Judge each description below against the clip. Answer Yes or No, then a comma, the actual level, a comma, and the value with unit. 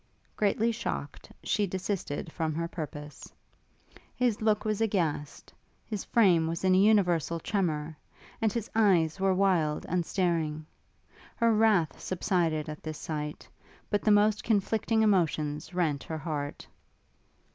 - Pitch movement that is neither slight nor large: Yes, average, 5.0 semitones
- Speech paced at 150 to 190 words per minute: No, slow, 135 wpm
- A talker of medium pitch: Yes, medium, 180 Hz